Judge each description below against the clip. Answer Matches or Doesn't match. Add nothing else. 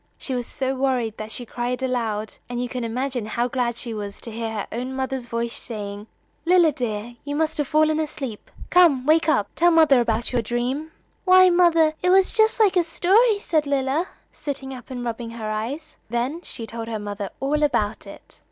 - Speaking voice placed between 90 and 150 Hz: Doesn't match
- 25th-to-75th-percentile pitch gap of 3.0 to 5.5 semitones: Matches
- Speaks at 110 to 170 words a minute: Doesn't match